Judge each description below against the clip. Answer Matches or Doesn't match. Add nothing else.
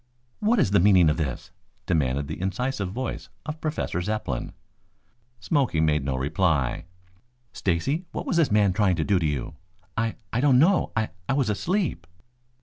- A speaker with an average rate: Matches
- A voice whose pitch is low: Matches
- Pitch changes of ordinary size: Doesn't match